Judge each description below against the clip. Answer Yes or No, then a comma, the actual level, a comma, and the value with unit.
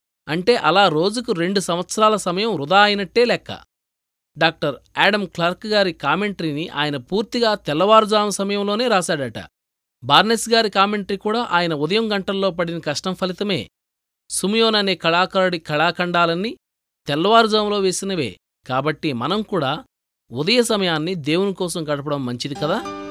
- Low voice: No, medium, 180 Hz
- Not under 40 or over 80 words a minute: No, average, 115 wpm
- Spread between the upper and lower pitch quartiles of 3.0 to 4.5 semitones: No, wide, 5.6 semitones